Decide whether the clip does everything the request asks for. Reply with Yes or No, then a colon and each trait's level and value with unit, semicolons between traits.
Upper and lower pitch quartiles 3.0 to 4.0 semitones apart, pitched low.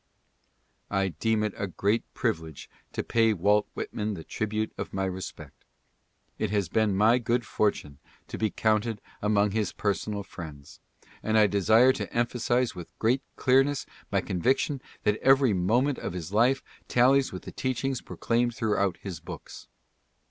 Yes: average, 3.7 semitones; low, 110 Hz